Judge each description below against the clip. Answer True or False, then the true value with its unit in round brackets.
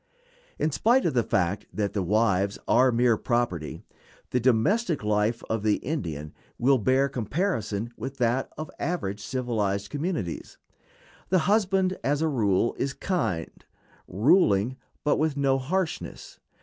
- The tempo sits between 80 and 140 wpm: True (135 wpm)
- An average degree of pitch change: False (6.7 semitones)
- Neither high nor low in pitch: False (125 Hz)